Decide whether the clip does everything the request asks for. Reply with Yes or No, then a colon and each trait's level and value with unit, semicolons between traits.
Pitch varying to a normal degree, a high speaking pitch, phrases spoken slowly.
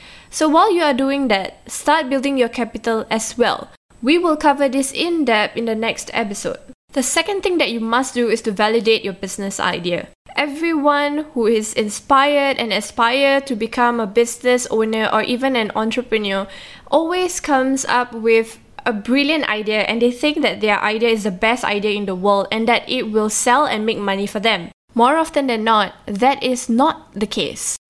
No: average, 4.0 semitones; high, 235 Hz; average, 190 wpm